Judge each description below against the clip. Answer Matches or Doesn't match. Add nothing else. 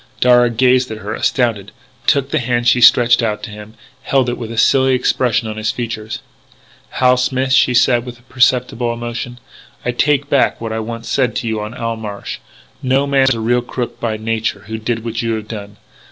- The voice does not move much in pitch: Matches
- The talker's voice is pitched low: Matches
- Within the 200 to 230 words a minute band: Matches